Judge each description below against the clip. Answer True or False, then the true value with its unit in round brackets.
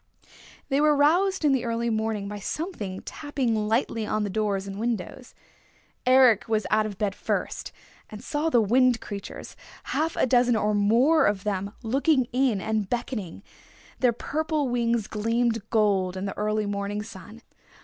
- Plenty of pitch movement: False (3.7 semitones)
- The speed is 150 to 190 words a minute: True (160 wpm)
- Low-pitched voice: False (225 Hz)